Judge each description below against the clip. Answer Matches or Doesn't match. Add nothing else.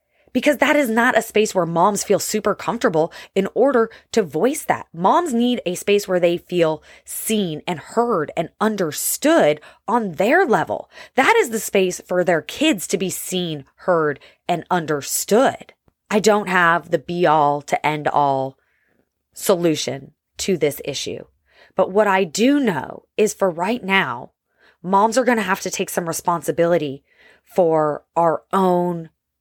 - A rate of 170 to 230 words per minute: Doesn't match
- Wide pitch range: Doesn't match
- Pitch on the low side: Doesn't match